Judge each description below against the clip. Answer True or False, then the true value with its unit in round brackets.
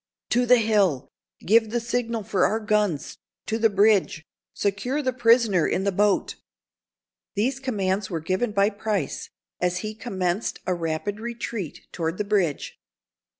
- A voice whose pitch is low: False (205 Hz)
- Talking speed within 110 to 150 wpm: True (140 wpm)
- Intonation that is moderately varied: True (3.5 semitones)